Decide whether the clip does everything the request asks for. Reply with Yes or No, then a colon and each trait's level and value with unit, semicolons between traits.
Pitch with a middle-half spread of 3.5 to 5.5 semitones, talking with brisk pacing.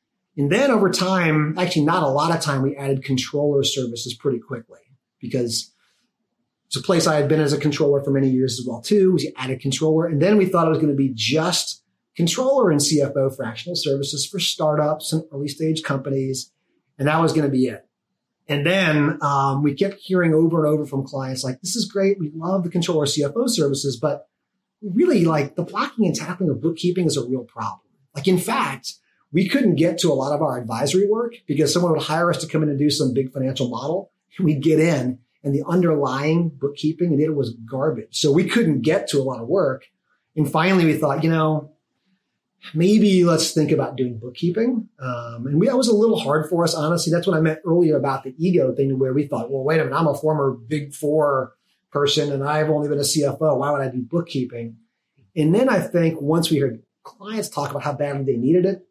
Yes: average, 4.0 semitones; fast, 220 wpm